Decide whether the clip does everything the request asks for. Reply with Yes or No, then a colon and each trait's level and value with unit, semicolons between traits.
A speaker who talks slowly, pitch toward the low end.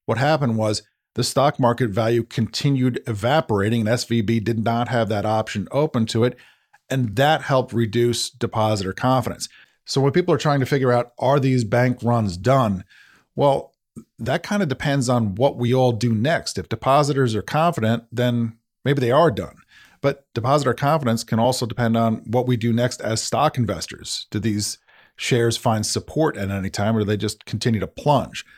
No: average, 185 wpm; low, 120 Hz